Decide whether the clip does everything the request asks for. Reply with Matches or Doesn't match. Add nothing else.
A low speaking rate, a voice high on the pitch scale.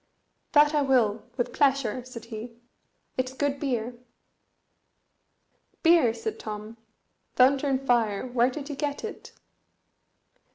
Matches